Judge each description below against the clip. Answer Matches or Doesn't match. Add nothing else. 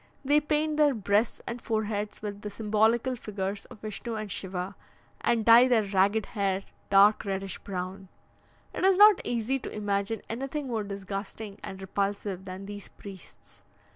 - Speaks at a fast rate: Doesn't match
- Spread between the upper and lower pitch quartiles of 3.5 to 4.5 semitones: Doesn't match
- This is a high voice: Matches